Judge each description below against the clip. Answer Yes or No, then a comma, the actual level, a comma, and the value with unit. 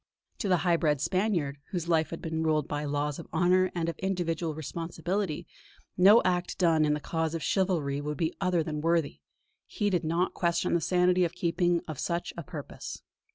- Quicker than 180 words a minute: Yes, average, 200 wpm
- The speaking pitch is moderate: Yes, medium, 170 Hz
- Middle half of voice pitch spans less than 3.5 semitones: Yes, narrow, 2.4 semitones